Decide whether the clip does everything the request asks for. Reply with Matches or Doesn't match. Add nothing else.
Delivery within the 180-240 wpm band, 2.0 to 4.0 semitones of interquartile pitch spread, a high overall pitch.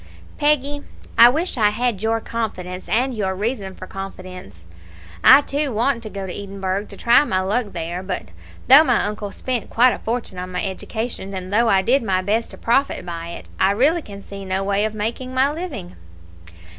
Doesn't match